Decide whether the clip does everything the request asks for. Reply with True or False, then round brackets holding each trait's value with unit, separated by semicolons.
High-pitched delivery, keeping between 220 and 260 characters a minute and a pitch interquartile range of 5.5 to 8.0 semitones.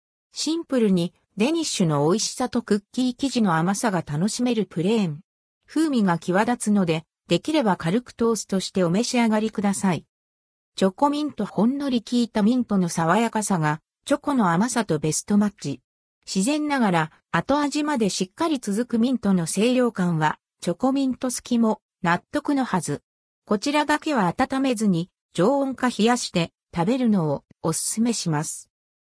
False (215 Hz; 340 characters per minute; 6.2 semitones)